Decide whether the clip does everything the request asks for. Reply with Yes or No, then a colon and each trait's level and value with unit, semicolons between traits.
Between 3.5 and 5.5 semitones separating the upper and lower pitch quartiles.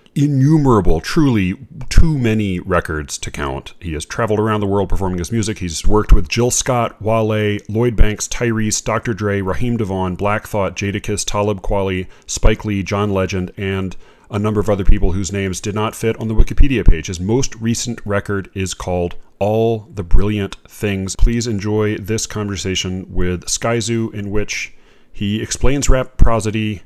No: average, 2.8 semitones